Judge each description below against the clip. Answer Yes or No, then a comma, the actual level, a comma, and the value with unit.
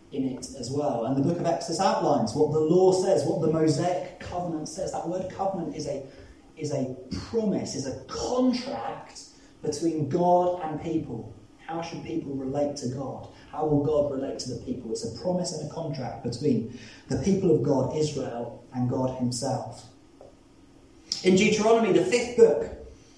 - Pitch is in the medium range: Yes, medium, 155 Hz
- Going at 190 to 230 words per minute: No, average, 175 wpm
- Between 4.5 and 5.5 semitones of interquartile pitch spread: Yes, average, 4.8 semitones